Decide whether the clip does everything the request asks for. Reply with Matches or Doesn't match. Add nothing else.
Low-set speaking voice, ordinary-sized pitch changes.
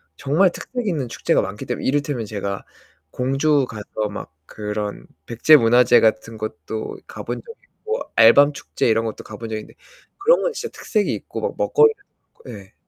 Doesn't match